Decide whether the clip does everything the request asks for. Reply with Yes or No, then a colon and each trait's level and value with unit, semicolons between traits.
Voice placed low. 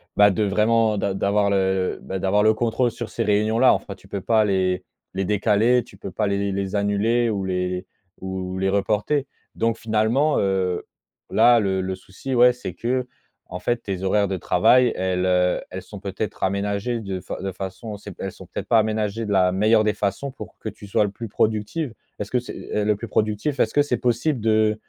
Yes: low, 105 Hz